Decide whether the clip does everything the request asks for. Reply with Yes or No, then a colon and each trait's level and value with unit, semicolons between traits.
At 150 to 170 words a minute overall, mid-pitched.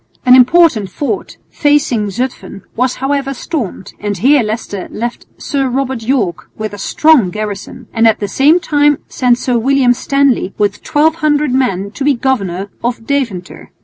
No: average, 155 wpm; very high, 250 Hz